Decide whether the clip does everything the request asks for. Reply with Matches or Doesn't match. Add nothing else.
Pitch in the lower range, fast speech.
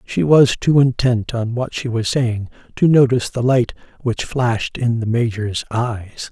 Doesn't match